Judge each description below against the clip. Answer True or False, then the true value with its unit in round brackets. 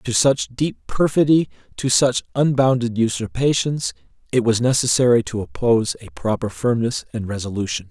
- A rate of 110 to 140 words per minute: True (135 wpm)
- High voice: False (120 Hz)